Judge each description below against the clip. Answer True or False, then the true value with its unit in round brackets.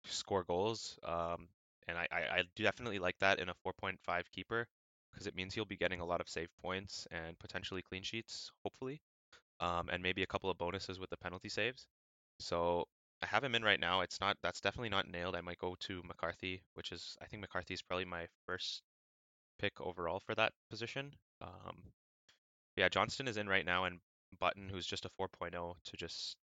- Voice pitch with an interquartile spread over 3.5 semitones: False (2.8 semitones)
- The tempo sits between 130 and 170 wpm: False (200 wpm)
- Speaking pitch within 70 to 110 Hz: True (95 Hz)